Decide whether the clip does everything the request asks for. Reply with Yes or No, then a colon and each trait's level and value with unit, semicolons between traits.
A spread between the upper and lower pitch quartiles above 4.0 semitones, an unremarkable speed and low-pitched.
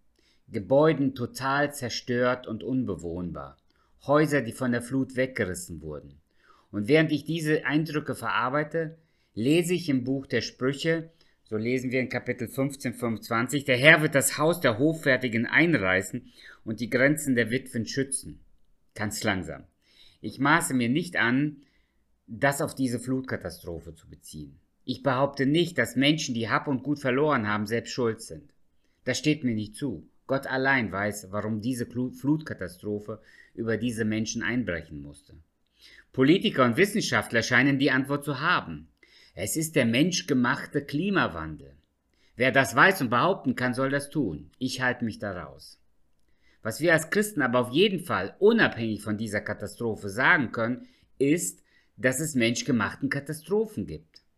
Yes: average, 4.7 semitones; average, 150 wpm; low, 125 Hz